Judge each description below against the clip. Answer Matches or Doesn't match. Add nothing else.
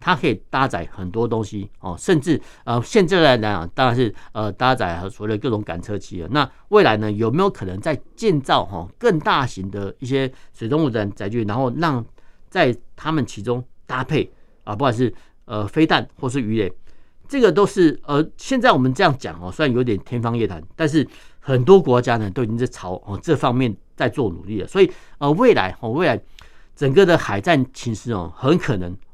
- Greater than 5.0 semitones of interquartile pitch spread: Matches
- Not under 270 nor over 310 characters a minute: Matches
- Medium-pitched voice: Doesn't match